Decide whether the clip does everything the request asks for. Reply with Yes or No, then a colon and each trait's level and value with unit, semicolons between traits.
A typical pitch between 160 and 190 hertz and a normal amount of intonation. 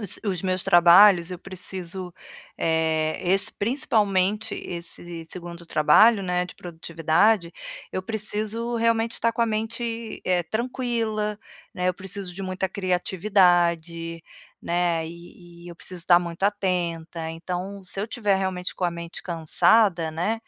Yes: medium, 185 Hz; average, 3.5 semitones